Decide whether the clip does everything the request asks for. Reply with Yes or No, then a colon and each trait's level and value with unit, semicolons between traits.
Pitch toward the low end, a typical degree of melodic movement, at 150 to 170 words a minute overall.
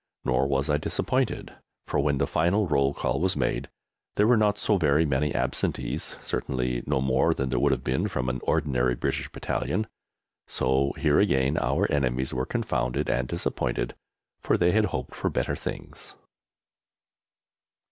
Yes: very low, 70 Hz; average, 3.2 semitones; average, 160 wpm